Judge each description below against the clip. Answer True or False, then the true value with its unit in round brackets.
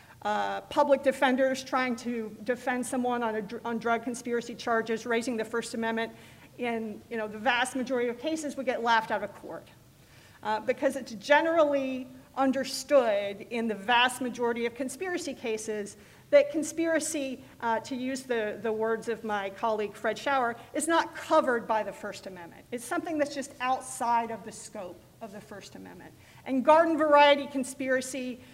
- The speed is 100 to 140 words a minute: False (165 wpm)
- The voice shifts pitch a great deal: False (3.2 semitones)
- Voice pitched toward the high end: True (245 Hz)